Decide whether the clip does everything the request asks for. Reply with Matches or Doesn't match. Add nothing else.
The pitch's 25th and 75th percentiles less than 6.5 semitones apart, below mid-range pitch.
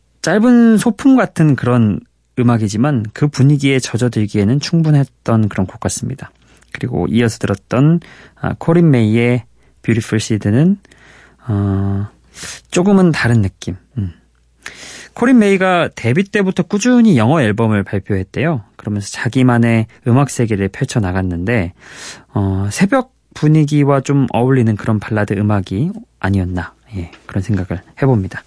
Doesn't match